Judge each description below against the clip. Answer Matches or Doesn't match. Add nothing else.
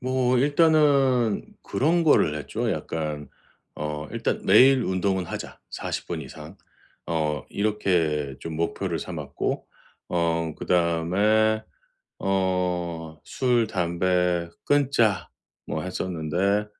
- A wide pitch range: Matches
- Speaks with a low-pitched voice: Matches